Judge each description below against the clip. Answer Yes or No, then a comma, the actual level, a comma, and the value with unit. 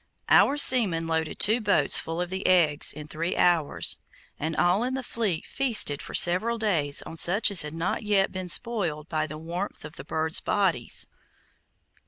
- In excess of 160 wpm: Yes, average, 180 wpm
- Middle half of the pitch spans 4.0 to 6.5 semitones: Yes, average, 4.7 semitones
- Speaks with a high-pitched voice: No, medium, 175 Hz